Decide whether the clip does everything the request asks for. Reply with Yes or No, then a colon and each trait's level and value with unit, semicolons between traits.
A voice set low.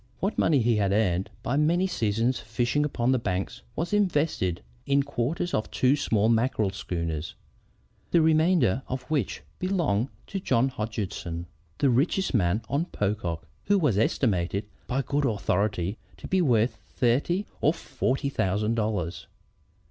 Yes: low, 120 Hz